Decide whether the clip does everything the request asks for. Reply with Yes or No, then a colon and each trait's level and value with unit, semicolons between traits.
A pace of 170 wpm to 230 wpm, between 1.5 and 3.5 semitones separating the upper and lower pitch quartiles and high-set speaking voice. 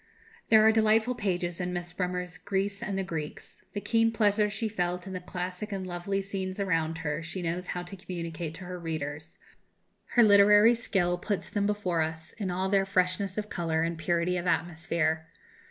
No: average, 185 wpm; average, 2.9 semitones; medium, 180 Hz